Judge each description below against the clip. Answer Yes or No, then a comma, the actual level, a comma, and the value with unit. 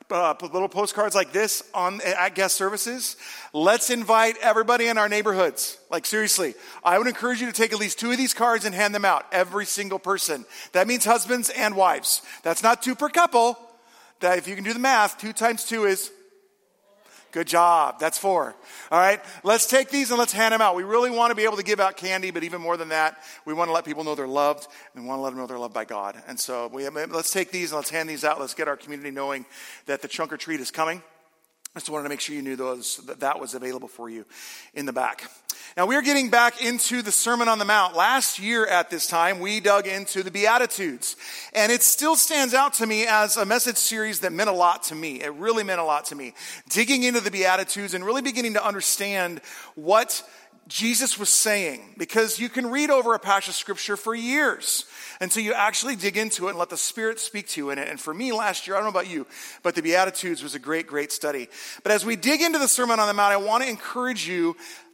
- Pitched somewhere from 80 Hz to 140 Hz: No, high, 200 Hz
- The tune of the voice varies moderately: No, wide, 5.7 semitones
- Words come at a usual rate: No, fast, 245 wpm